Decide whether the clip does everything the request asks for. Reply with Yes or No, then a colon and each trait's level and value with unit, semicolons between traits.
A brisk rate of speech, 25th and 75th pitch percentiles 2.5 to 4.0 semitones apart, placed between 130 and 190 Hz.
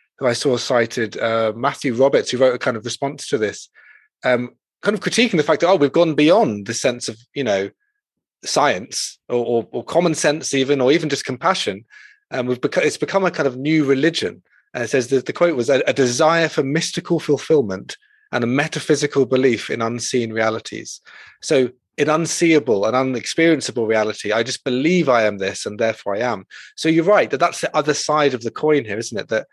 No: fast, 210 wpm; average, 4.8 semitones; medium, 140 Hz